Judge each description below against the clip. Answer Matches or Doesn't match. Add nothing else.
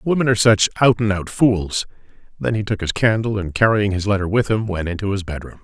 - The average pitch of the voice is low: Matches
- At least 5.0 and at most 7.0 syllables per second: Matches